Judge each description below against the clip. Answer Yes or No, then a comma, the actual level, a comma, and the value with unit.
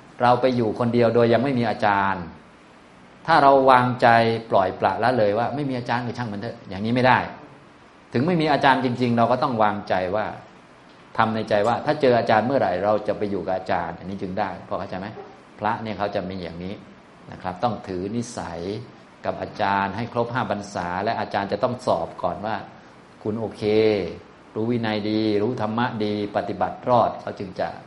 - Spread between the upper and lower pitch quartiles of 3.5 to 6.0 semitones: No, average, 3.1 semitones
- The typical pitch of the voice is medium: No, low, 110 Hz